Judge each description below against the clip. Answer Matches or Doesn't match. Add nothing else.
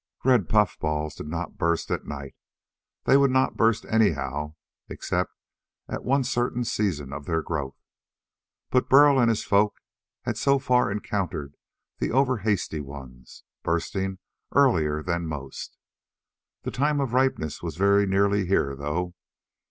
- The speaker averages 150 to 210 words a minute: Doesn't match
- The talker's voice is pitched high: Doesn't match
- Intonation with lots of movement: Matches